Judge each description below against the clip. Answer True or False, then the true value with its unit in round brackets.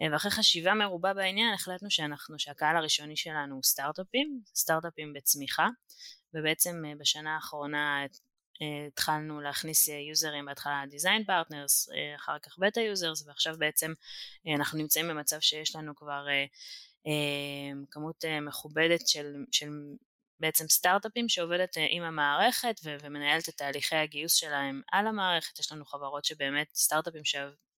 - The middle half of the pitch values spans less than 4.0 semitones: True (2.6 semitones)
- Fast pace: False (125 wpm)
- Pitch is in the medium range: True (155 Hz)